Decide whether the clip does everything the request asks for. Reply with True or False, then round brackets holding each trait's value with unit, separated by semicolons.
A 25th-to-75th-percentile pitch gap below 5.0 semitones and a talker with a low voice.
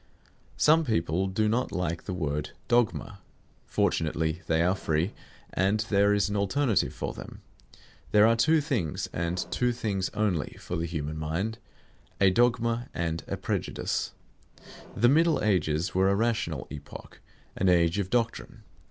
False (5.4 semitones; 100 Hz)